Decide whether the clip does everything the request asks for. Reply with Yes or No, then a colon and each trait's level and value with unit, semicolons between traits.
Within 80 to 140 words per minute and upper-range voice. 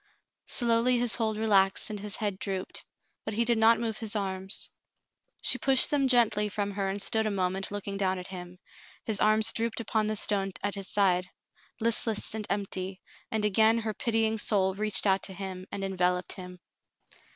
No: average, 185 wpm; high, 205 Hz